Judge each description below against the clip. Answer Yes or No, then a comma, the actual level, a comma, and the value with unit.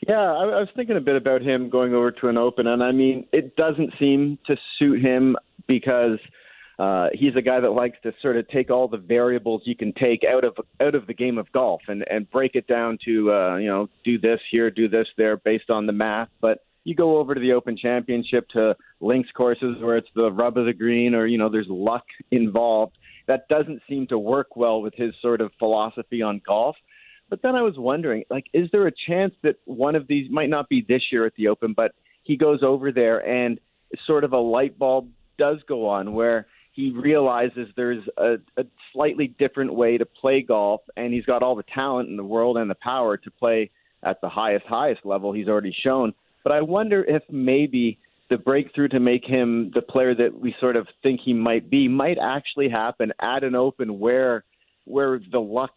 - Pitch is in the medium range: No, low, 125 Hz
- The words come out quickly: Yes, fast, 220 wpm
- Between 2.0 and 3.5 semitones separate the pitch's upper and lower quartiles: Yes, average, 2.9 semitones